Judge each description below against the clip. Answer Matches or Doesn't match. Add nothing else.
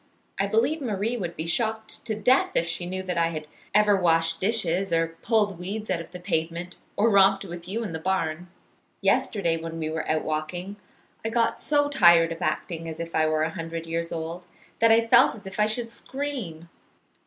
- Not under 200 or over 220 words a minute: Matches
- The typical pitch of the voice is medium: Matches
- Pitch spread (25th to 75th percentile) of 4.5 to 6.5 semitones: Matches